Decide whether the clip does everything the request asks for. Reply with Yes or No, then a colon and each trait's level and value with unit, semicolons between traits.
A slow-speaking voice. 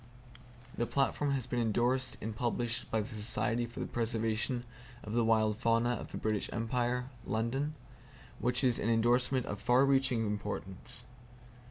No: average, 155 wpm